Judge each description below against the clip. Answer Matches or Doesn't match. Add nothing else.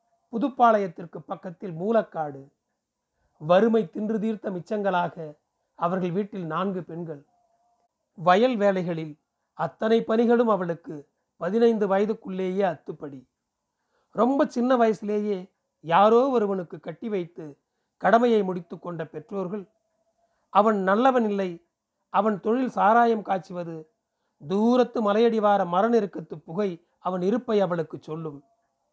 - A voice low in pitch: Doesn't match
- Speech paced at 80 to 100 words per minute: Matches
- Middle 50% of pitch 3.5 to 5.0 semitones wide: Matches